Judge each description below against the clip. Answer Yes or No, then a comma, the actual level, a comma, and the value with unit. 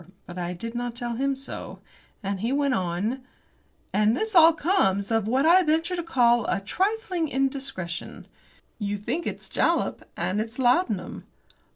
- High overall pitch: Yes, high, 245 Hz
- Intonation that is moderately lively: No, wide, 7.4 semitones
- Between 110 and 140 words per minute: No, average, 160 wpm